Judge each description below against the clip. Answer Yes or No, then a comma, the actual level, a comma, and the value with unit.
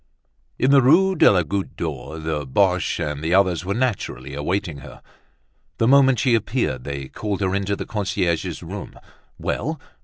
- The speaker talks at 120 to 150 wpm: No, average, 165 wpm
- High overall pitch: No, very low, 95 Hz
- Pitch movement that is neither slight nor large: No, wide, 6.4 semitones